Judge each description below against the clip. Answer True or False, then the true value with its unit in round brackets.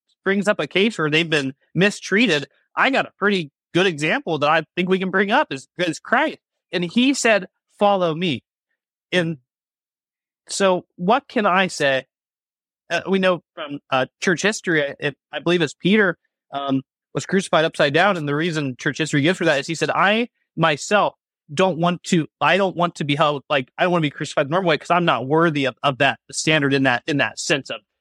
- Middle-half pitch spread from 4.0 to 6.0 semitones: True (4.5 semitones)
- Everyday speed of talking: False (210 wpm)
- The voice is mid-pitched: True (170 Hz)